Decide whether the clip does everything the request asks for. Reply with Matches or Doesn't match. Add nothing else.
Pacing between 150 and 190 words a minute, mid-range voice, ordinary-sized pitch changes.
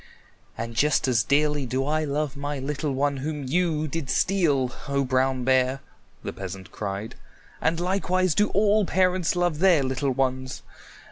Matches